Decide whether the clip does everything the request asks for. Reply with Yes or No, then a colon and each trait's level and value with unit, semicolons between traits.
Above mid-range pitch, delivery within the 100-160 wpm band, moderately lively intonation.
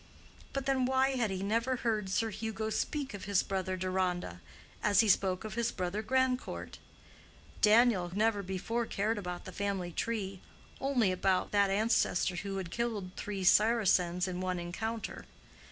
Yes: high, 205 Hz; average, 155 wpm; average, 3.6 semitones